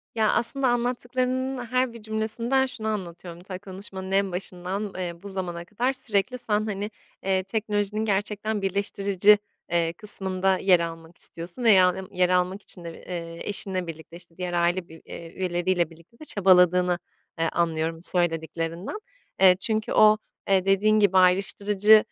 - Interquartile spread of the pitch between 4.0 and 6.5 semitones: No, average, 3.4 semitones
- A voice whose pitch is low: No, high, 190 Hz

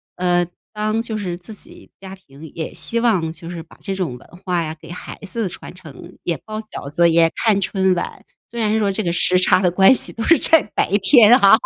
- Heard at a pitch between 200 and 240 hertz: No, high, 190 Hz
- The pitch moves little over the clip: No, average, 4.0 semitones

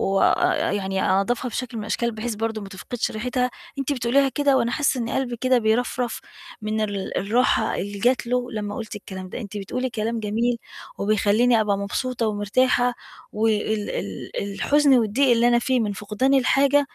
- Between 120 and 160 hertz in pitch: No, high, 230 Hz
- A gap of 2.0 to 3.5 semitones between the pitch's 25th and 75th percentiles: Yes, average, 3.1 semitones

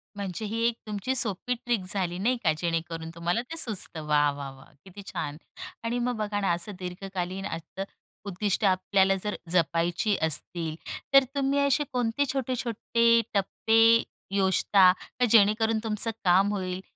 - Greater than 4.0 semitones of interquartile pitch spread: Yes, average, 4.5 semitones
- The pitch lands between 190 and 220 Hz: Yes, high, 200 Hz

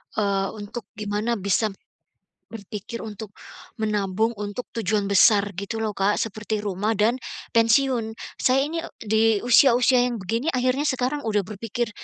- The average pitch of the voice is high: Yes, high, 220 Hz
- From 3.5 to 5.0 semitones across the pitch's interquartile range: No, narrow, 2.6 semitones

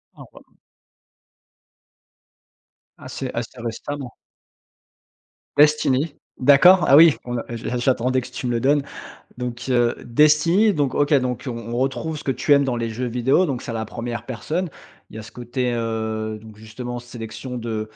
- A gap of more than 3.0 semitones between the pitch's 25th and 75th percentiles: Yes, average, 3.4 semitones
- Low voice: Yes, low, 125 Hz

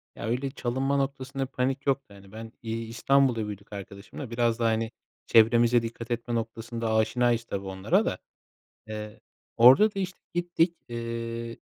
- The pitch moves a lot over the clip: No, average, 2.8 semitones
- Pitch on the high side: No, low, 115 Hz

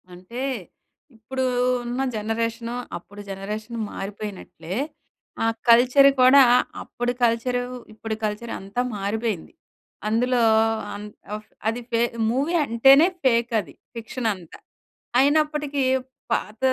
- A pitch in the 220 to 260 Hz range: Yes, high, 230 Hz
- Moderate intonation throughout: Yes, average, 3.2 semitones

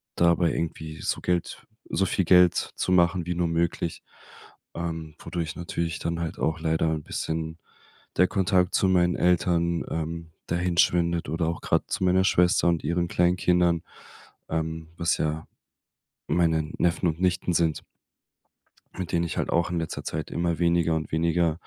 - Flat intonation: Yes, narrow, 1.4 semitones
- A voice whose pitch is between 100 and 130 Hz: No, very low, 85 Hz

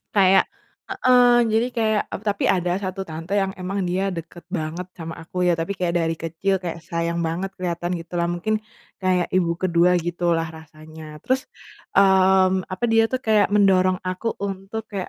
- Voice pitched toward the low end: No, medium, 185 Hz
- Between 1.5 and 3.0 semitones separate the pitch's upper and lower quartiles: Yes, narrow, 2.5 semitones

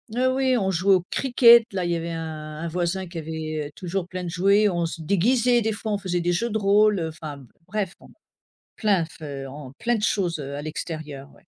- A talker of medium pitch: Yes, medium, 180 Hz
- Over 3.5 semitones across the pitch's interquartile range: Yes, average, 4.6 semitones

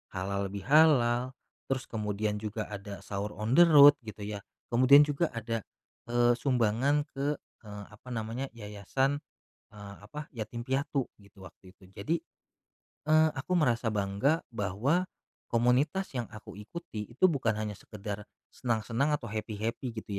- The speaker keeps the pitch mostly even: No, average, 4.8 semitones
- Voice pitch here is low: Yes, low, 115 Hz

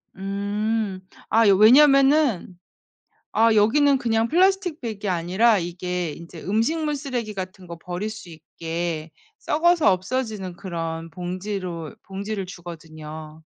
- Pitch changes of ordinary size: Yes, average, 4.8 semitones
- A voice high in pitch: Yes, high, 195 Hz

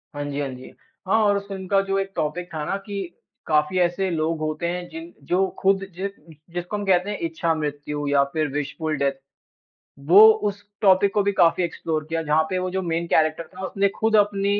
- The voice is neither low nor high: Yes, medium, 175 Hz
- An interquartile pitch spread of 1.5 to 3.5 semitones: No, average, 4.0 semitones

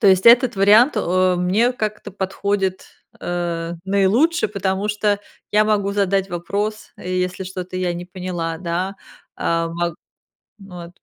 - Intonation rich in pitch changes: No, narrow, 2.4 semitones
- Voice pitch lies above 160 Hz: Yes, high, 190 Hz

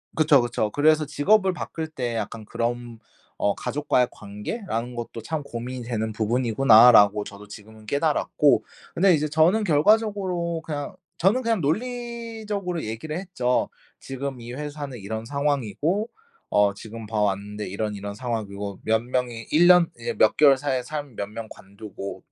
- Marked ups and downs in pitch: Yes, wide, 6.3 semitones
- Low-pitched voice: Yes, low, 125 Hz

